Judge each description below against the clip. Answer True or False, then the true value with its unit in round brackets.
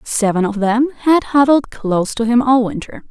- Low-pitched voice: False (240 Hz)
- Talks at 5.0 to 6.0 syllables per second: False (4.7 syllables/s)